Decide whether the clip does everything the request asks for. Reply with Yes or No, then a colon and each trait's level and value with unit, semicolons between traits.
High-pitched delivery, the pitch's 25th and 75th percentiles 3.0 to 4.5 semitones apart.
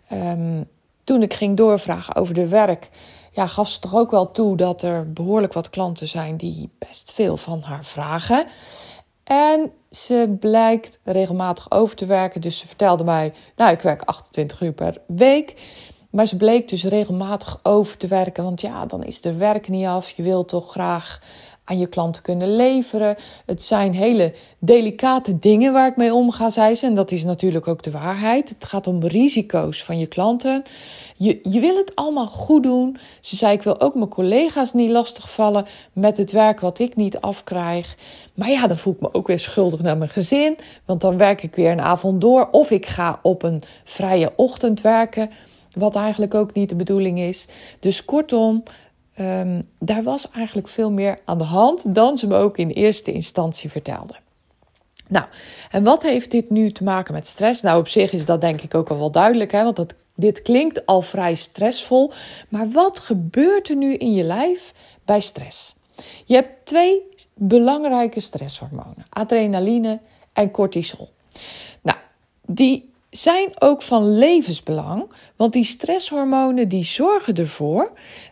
No: high, 205 Hz; average, 4.9 semitones